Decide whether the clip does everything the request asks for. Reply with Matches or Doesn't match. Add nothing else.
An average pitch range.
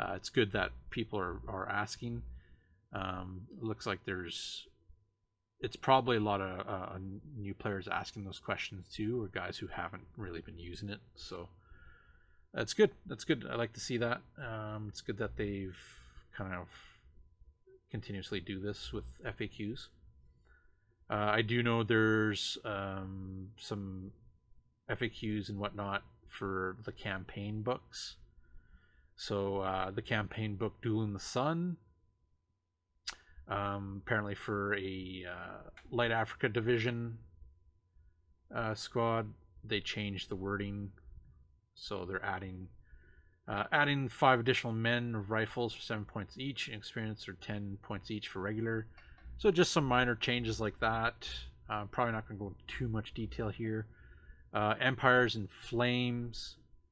Matches